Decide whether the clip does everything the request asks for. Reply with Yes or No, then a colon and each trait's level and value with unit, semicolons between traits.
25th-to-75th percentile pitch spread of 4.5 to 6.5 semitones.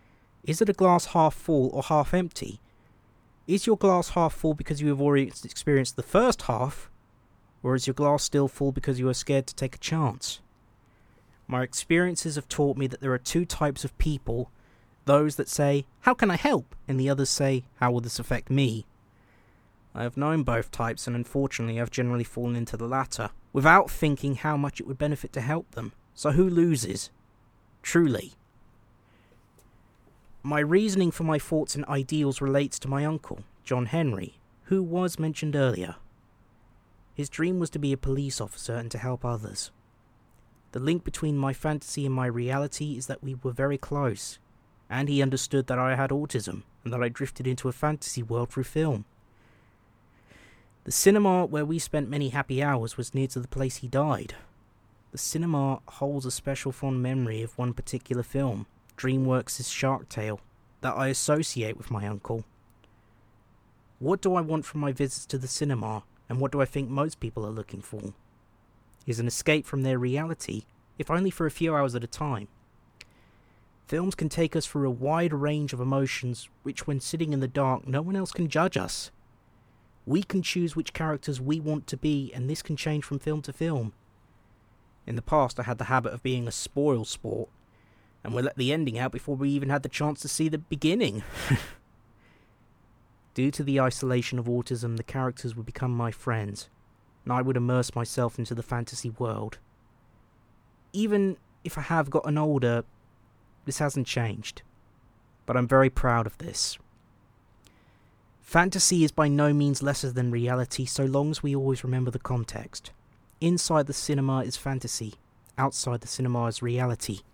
No: average, 3.9 semitones